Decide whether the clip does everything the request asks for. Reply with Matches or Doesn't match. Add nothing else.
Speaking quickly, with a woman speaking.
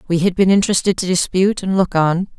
Matches